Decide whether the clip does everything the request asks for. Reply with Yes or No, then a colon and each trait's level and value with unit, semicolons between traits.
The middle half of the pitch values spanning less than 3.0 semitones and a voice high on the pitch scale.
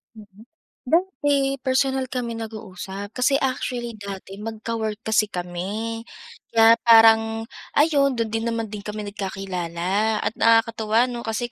Yes: narrow, 2.4 semitones; high, 225 Hz